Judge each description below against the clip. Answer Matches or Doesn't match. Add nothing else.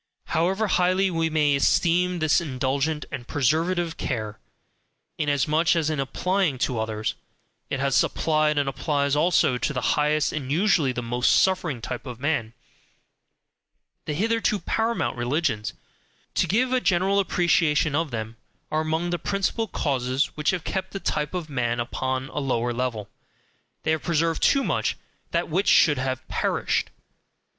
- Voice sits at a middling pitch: Matches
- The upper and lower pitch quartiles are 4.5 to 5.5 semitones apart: Matches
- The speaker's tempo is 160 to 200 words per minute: Doesn't match